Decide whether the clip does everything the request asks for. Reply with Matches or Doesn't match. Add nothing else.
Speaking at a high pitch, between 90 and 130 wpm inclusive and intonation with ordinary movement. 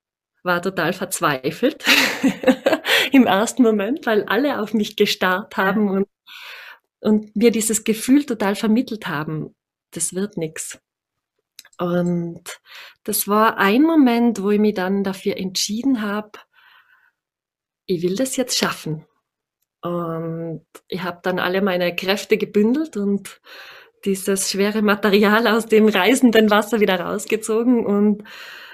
Matches